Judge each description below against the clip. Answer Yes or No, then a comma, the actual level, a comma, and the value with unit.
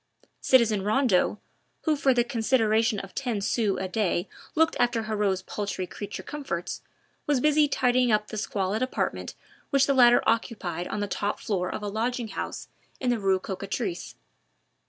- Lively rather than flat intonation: No, average, 4.1 semitones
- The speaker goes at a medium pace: Yes, average, 160 wpm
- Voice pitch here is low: No, high, 220 Hz